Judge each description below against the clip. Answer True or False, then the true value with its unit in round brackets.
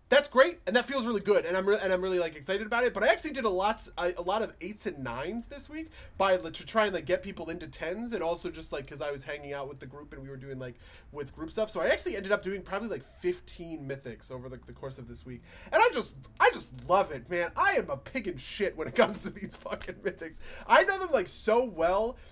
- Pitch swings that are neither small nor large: False (7.4 semitones)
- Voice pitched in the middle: True (180 Hz)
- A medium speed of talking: False (280 wpm)